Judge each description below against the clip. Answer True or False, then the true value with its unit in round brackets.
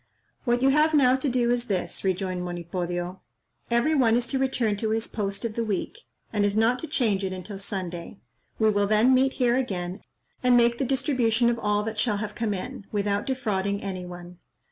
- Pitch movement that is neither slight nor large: True (4.1 semitones)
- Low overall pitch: False (215 Hz)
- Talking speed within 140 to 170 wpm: False (205 wpm)